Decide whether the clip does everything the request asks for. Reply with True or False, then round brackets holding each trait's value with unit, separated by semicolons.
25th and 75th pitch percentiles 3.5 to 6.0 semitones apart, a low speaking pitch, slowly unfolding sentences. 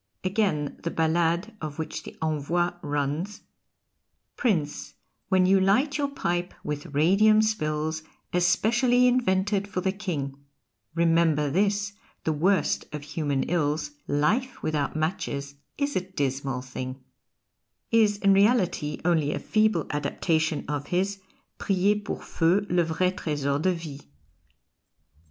False (5.1 semitones; 175 Hz; 125 wpm)